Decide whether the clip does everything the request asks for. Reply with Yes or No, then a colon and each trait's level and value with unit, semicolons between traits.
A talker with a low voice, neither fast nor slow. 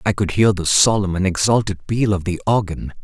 No: very low, 95 Hz; fast, 215 wpm